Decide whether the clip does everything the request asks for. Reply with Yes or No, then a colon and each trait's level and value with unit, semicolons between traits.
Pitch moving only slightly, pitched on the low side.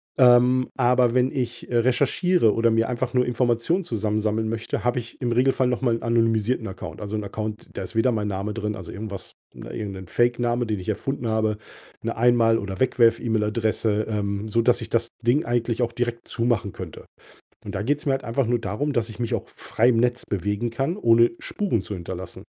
Yes: narrow, 2.3 semitones; low, 115 Hz